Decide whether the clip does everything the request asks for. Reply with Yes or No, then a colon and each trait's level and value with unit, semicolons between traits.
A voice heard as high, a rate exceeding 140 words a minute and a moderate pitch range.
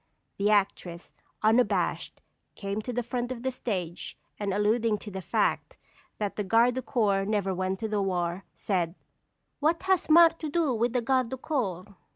Yes: high, 215 Hz; average, 175 wpm; average, 4.2 semitones